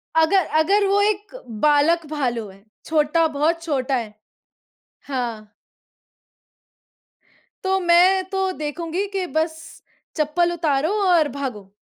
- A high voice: Yes, very high, 320 Hz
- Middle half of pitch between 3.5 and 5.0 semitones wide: Yes, average, 4.1 semitones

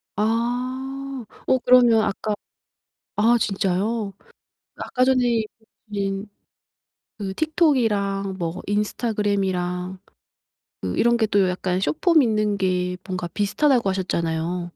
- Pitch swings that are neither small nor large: Yes, average, 4.3 semitones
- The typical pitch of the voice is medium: No, high, 205 Hz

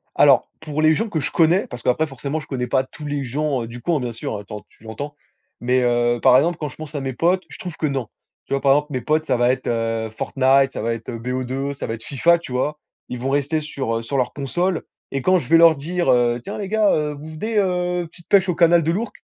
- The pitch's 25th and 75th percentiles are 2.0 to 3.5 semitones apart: No, average, 4.8 semitones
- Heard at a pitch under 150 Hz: Yes, medium, 140 Hz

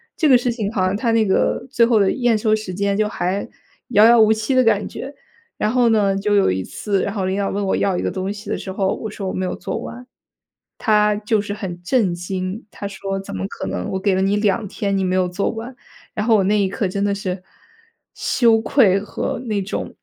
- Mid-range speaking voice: No, high, 205 Hz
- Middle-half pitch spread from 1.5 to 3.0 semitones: Yes, narrow, 2.4 semitones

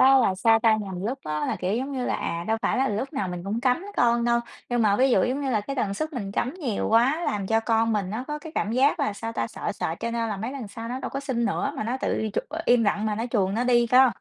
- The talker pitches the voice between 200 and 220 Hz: No, high, 230 Hz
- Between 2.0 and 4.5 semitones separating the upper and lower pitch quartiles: Yes, average, 3.8 semitones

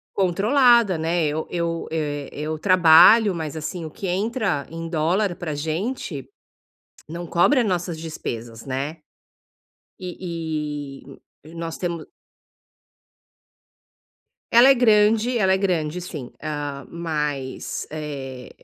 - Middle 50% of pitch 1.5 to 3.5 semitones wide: No, average, 3.9 semitones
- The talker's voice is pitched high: No, medium, 165 Hz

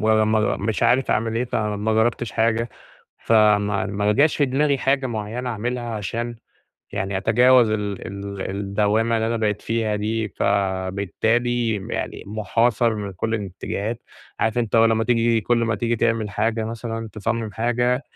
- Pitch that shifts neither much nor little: No, narrow, 2.2 semitones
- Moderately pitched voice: No, low, 110 Hz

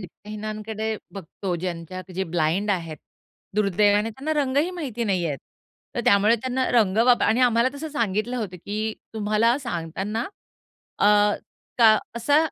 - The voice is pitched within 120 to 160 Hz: No, high, 215 Hz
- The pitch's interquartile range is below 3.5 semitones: No, average, 3.8 semitones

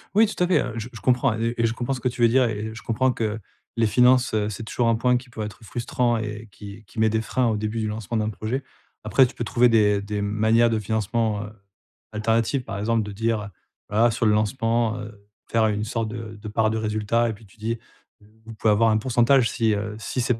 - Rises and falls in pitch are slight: Yes, narrow, 1.8 semitones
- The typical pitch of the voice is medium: No, low, 110 Hz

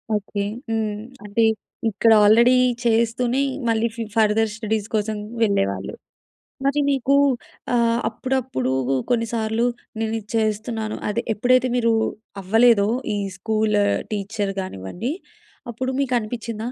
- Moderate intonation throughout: No, narrow, 2.0 semitones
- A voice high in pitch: Yes, high, 225 Hz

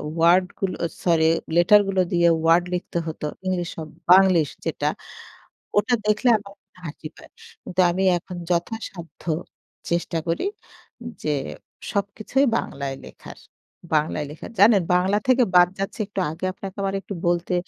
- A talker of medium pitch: Yes, medium, 180 Hz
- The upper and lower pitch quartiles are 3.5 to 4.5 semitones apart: No, average, 2.8 semitones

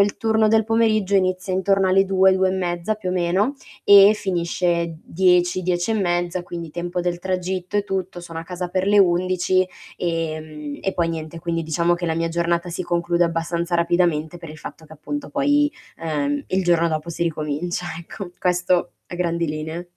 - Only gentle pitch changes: Yes, narrow, 2.0 semitones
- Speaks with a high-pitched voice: No, medium, 175 Hz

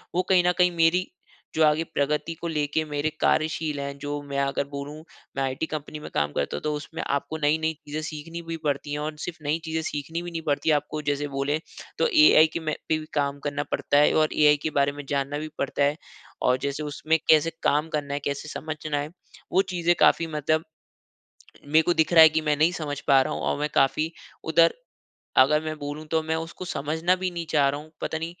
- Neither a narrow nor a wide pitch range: No, narrow, 1.9 semitones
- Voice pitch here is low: No, medium, 150 Hz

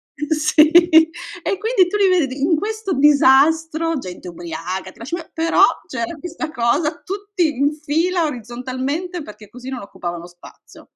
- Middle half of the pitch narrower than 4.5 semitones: No, average, 5.3 semitones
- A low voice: No, very high, 305 Hz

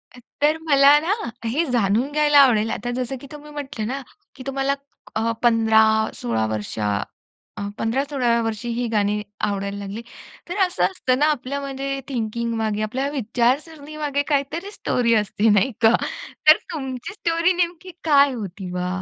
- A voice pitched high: Yes, very high, 255 Hz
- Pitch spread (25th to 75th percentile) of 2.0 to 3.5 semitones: No, average, 4.7 semitones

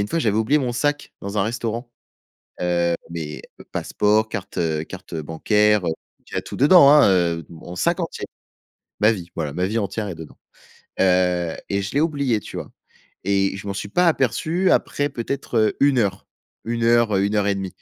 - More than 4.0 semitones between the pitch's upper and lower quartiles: Yes, average, 4.7 semitones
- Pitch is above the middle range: No, low, 105 Hz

